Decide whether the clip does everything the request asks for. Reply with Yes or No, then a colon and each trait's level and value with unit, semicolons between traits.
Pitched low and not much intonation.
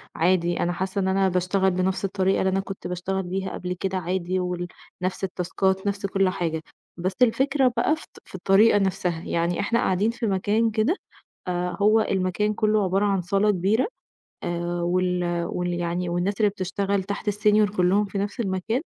No: high, 190 Hz; narrow, 2.2 semitones